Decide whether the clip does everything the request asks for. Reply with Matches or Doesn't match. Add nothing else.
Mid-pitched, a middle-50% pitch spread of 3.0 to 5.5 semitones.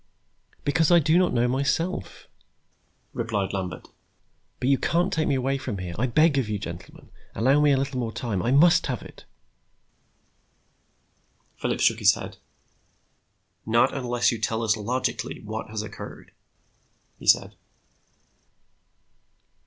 Doesn't match